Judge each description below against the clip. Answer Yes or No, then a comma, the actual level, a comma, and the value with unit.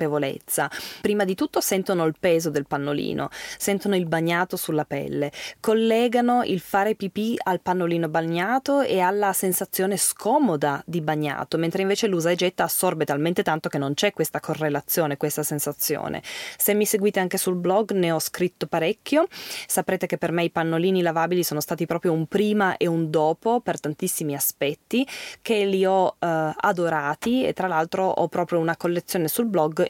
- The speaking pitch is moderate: Yes, medium, 175 Hz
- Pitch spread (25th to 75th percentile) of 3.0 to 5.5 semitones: Yes, average, 3.8 semitones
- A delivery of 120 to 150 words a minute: No, average, 165 wpm